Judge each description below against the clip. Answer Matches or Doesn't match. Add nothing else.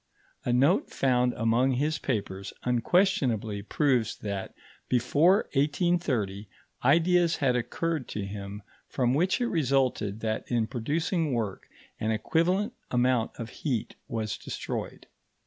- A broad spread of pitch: Matches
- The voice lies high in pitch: Doesn't match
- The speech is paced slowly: Matches